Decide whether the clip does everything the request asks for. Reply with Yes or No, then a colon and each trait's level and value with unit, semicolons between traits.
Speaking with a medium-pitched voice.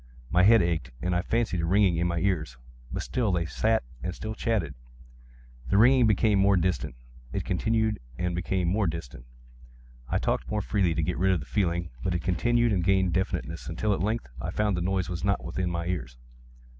No: very low, 90 Hz